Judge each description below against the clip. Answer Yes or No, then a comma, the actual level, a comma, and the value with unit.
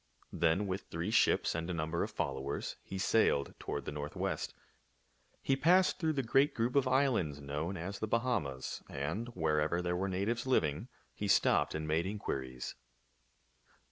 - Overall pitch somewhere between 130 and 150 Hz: No, very low, 90 Hz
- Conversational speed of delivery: Yes, average, 160 wpm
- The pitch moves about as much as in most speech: No, wide, 7.0 semitones